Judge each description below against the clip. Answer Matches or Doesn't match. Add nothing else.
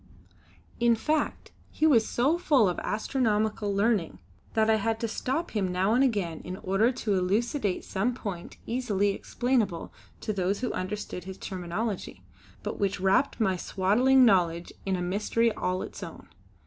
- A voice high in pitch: Matches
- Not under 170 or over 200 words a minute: Doesn't match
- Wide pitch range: Doesn't match